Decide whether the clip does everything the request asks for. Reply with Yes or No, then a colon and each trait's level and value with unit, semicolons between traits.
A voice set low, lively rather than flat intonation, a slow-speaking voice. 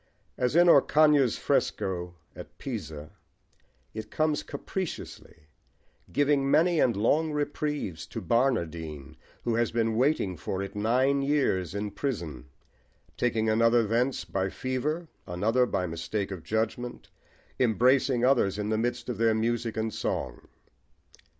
Yes: low, 115 Hz; wide, 5.7 semitones; slow, 130 wpm